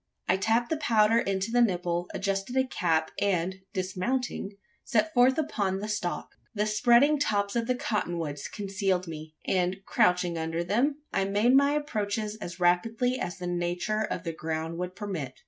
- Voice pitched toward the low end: No, high, 195 Hz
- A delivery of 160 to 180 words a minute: Yes, average, 170 wpm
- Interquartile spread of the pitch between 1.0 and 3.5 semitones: No, average, 4.6 semitones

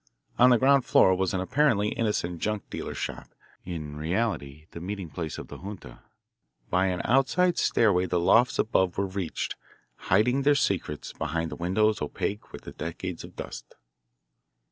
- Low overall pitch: Yes, very low, 95 Hz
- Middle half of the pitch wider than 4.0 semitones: Yes, average, 4.6 semitones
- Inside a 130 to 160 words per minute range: Yes, average, 155 wpm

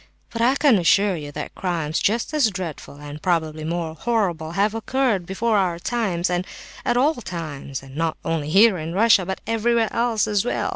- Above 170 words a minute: Yes, average, 190 wpm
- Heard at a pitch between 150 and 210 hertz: Yes, high, 190 Hz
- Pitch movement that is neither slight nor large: No, wide, 5.8 semitones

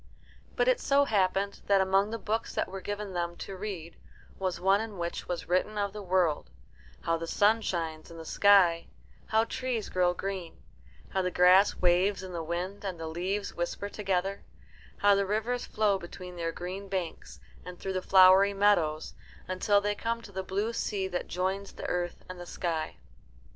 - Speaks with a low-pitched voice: No, high, 190 Hz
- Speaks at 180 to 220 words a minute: Yes, average, 185 wpm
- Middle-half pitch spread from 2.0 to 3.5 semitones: Yes, narrow, 2.4 semitones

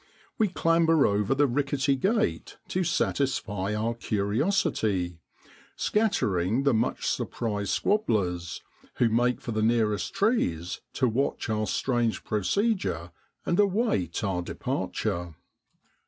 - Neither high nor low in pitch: No, low, 115 Hz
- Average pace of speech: No, slow, 110 wpm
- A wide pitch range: Yes, wide, 8.3 semitones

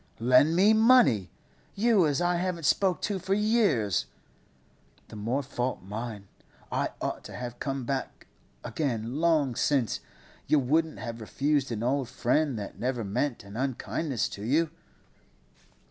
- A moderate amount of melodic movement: No, wide, 5.9 semitones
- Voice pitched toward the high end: No, low, 135 Hz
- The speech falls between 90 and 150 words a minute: Yes, average, 145 wpm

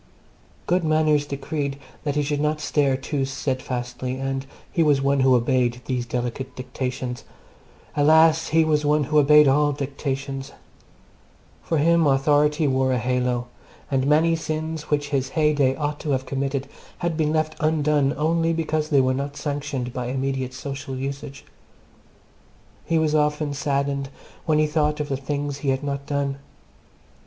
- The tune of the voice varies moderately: No, narrow, 2.3 semitones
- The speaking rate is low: No, average, 155 wpm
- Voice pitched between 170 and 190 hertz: No, medium, 140 Hz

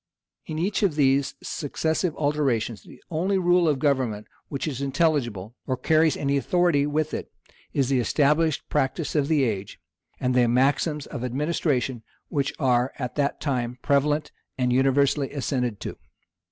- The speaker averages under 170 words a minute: Yes, average, 155 wpm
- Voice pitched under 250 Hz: Yes, medium, 140 Hz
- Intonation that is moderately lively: Yes, average, 3.4 semitones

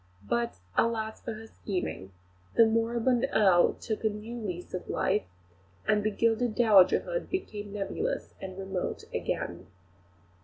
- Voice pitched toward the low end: No, high, 215 Hz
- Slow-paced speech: Yes, slow, 125 wpm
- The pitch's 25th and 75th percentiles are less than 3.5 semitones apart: Yes, average, 2.8 semitones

